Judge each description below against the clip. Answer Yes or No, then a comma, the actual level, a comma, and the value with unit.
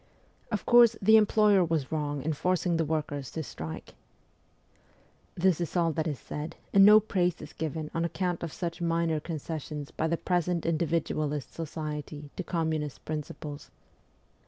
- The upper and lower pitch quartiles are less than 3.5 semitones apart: Yes, average, 2.7 semitones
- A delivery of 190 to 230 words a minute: No, average, 160 wpm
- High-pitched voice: No, medium, 160 Hz